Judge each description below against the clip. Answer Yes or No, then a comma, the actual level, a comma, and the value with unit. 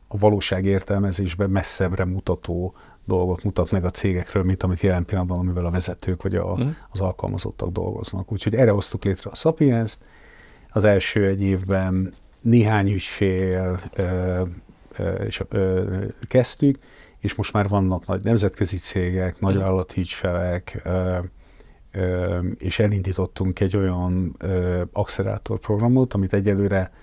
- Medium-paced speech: Yes, average, 120 wpm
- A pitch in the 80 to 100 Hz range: Yes, very low, 95 Hz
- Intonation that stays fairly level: Yes, narrow, 2.1 semitones